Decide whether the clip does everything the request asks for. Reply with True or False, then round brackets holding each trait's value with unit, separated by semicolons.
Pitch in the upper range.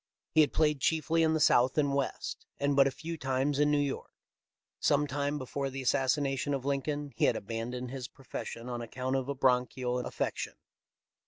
False (135 Hz)